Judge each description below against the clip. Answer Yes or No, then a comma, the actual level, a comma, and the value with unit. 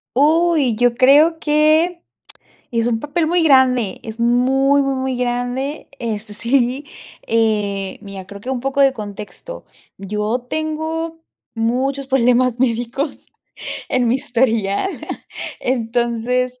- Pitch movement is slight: No, average, 3.6 semitones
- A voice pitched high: Yes, very high, 250 Hz